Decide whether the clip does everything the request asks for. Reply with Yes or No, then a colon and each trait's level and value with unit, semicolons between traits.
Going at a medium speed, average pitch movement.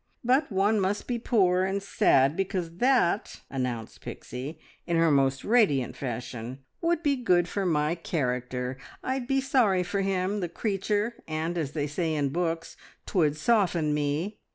No: average, 155 wpm; wide, 6.0 semitones